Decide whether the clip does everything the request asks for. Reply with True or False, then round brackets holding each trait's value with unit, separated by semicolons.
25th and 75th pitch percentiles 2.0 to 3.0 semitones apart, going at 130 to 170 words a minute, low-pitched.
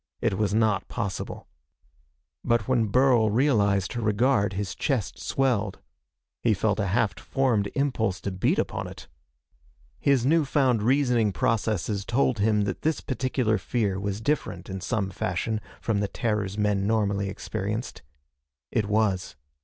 False (3.7 semitones; 145 wpm; 110 Hz)